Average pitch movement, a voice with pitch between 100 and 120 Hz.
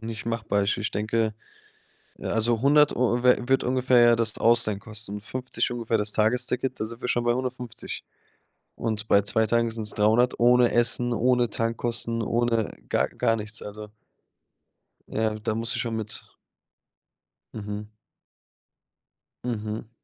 No: narrow, 2.1 semitones; low, 115 Hz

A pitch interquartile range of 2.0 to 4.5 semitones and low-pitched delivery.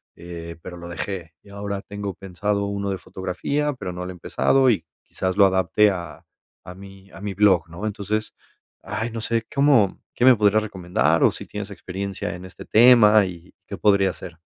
Yes: average, 2.7 semitones; low, 100 Hz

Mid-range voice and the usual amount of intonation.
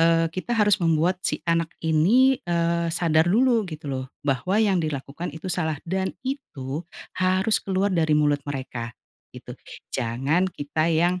Yes: medium, 165 Hz; average, 3.7 semitones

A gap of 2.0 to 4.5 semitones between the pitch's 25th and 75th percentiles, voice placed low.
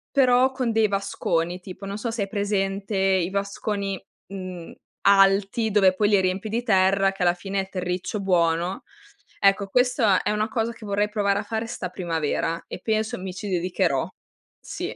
No: narrow, 2.5 semitones; high, 195 Hz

